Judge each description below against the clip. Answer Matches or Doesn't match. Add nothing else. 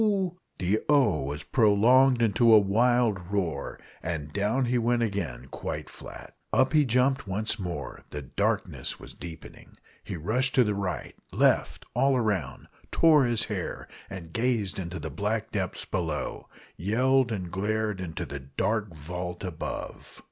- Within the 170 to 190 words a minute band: Doesn't match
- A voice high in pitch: Doesn't match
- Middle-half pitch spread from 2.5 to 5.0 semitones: Doesn't match